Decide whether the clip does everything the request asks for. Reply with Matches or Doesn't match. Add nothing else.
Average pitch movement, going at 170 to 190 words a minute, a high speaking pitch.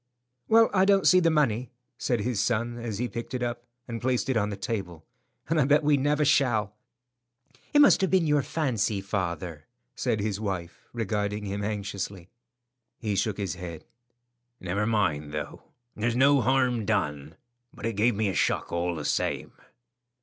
Doesn't match